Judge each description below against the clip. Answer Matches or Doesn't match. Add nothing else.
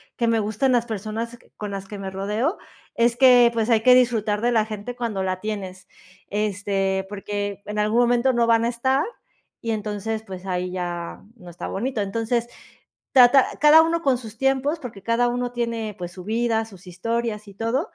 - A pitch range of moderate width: Matches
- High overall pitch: Matches